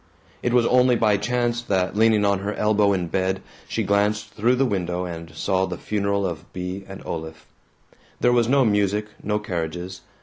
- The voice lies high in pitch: No, low, 100 Hz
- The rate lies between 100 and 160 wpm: No, average, 180 wpm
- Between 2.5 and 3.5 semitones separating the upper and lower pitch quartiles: Yes, average, 3.0 semitones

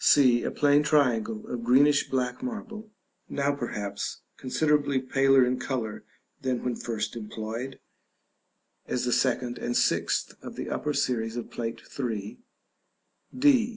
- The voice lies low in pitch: Yes, low, 125 Hz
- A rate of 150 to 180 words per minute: No, slow, 135 wpm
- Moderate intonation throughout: Yes, average, 3.3 semitones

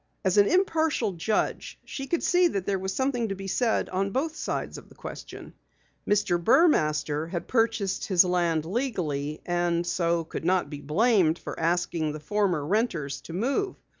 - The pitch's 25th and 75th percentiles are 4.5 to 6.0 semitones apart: Yes, wide, 5.5 semitones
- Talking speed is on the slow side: No, average, 170 wpm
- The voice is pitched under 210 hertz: Yes, medium, 185 Hz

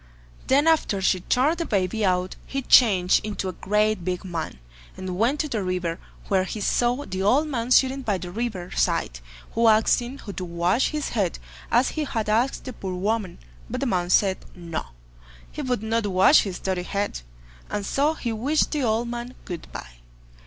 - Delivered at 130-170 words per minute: No, average, 190 wpm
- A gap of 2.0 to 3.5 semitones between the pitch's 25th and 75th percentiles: No, average, 5.1 semitones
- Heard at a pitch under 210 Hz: No, high, 215 Hz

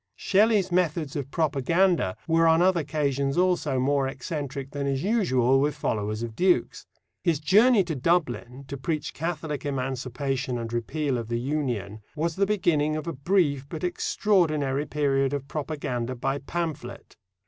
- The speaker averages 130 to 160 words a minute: Yes, average, 150 wpm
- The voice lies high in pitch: No, medium, 145 Hz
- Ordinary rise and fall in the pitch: Yes, average, 4.1 semitones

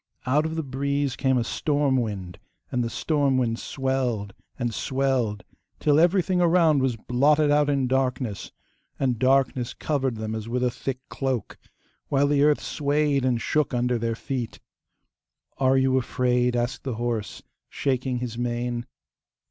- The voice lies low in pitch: Yes, low, 130 Hz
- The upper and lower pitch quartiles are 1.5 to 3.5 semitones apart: Yes, average, 2.7 semitones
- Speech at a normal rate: Yes, average, 155 wpm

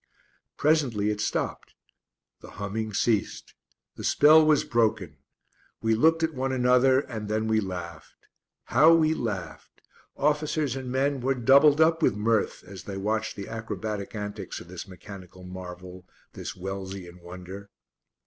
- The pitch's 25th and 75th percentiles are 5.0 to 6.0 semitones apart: Yes, wide, 5.6 semitones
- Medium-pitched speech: No, low, 110 Hz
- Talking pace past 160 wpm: No, average, 140 wpm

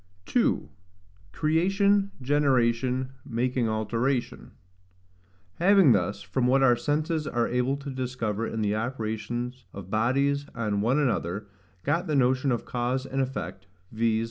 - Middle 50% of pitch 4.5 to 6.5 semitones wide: No, average, 3.5 semitones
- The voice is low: Yes, low, 125 Hz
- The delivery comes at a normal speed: No, slow, 130 wpm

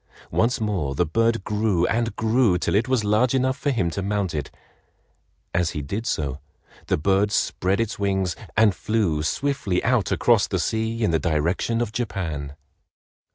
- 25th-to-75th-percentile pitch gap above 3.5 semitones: Yes, average, 4.8 semitones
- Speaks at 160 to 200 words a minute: Yes, average, 170 wpm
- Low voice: Yes, low, 105 Hz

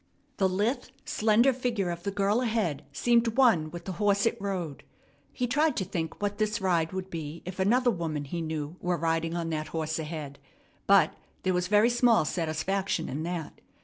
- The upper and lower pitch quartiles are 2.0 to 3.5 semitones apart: No, average, 4.8 semitones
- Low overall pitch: No, medium, 185 Hz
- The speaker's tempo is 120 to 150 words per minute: No, average, 185 wpm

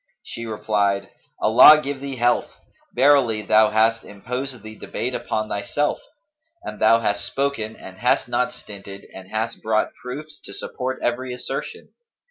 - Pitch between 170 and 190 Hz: No, low, 115 Hz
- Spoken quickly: No, average, 145 wpm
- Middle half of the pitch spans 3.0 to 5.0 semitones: Yes, average, 3.5 semitones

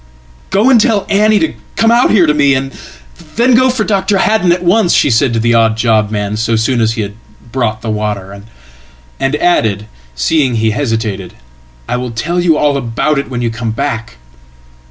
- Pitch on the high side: No, low, 125 Hz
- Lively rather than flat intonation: Yes, wide, 8.1 semitones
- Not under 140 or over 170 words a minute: No, average, 180 wpm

